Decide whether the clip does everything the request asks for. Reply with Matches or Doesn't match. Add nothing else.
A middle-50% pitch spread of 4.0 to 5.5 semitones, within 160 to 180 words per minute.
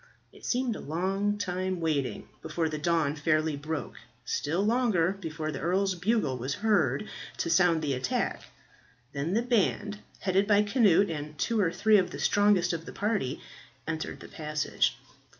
Matches